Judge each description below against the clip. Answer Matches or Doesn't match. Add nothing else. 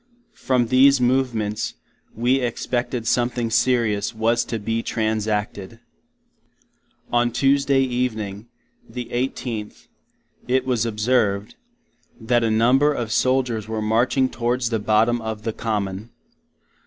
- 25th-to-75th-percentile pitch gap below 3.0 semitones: Matches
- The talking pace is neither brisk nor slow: Doesn't match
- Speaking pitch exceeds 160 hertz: Doesn't match